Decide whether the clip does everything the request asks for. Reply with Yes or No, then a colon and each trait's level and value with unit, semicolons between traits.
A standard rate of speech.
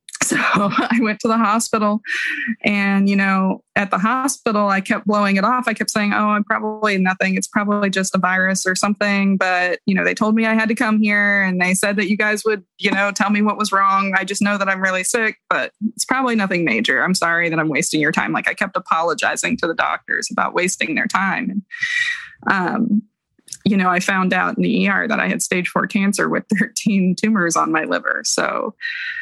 No: fast, 225 wpm